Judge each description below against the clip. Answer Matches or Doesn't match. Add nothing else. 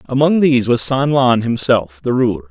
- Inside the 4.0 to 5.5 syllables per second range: Matches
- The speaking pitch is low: Matches